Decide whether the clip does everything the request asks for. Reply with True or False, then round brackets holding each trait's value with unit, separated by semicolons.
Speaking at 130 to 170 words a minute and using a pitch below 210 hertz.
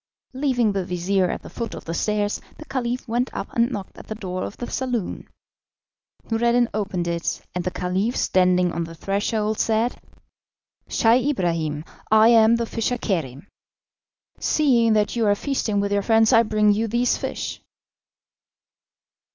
False (160 wpm; 215 Hz)